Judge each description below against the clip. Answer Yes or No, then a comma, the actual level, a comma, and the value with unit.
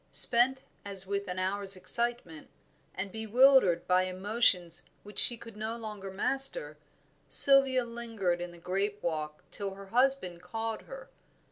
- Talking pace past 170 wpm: No, average, 140 wpm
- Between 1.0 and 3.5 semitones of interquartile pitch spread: No, average, 4.4 semitones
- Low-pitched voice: No, high, 200 Hz